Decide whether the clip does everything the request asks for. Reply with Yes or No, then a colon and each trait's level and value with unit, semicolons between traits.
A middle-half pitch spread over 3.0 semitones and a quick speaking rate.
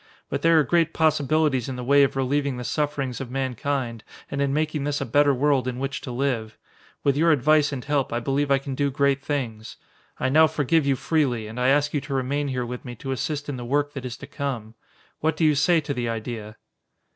No: narrow, 2.6 semitones; fast, 235 wpm